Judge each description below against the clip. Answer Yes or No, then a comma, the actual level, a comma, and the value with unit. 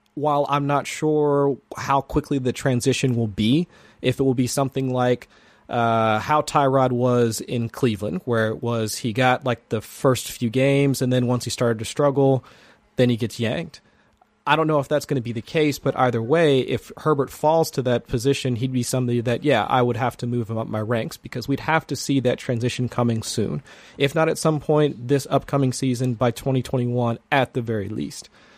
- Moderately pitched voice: No, low, 130 Hz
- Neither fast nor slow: No, fast, 210 wpm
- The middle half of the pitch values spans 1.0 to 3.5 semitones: Yes, average, 2.8 semitones